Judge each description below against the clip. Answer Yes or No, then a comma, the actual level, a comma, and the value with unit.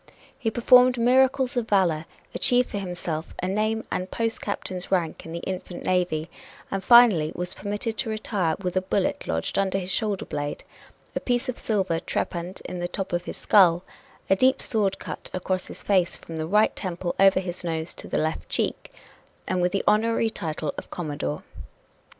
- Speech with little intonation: No, average, 4.0 semitones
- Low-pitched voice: No, high, 190 Hz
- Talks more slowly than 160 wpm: No, average, 185 wpm